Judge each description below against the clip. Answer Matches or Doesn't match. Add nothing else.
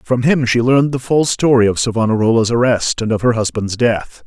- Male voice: Matches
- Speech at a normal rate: Doesn't match